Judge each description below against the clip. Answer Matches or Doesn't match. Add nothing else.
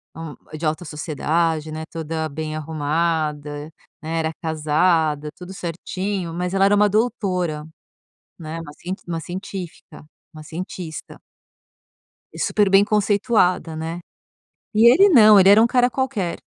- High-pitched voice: Doesn't match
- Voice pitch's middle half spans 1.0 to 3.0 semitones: Doesn't match